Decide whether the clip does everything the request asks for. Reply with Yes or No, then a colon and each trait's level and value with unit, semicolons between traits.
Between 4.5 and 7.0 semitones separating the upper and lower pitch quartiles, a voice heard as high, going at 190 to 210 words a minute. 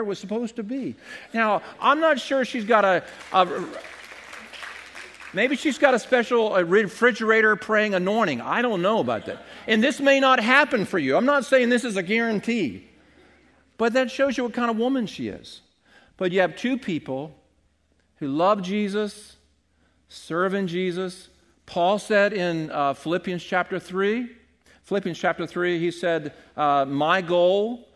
No: wide, 5.4 semitones; high, 205 Hz; average, 160 wpm